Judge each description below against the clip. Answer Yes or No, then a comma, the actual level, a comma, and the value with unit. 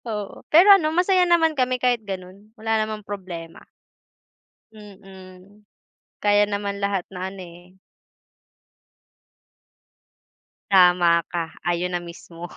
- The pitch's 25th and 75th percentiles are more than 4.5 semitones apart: No, average, 3.4 semitones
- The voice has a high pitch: Yes, high, 200 Hz